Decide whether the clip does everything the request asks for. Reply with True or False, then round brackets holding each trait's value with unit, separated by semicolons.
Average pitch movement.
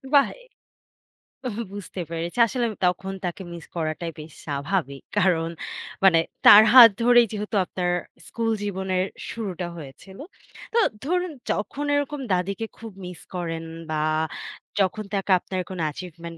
True (4.2 semitones)